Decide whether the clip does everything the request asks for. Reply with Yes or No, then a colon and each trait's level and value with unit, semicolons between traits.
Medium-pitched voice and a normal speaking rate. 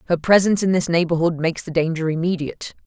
Yes: medium, 170 Hz; average, 190 wpm